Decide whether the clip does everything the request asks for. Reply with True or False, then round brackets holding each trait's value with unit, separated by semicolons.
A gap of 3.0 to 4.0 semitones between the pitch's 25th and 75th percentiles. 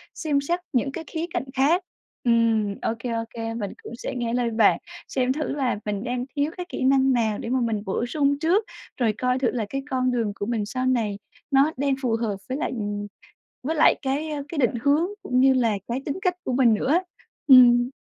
True (3.5 semitones)